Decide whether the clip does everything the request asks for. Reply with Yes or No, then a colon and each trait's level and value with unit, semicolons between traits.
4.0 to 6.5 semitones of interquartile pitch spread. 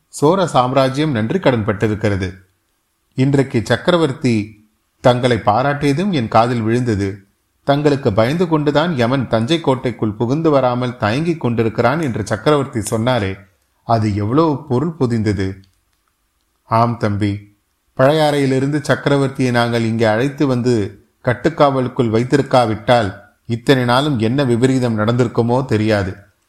Yes: average, 4.3 semitones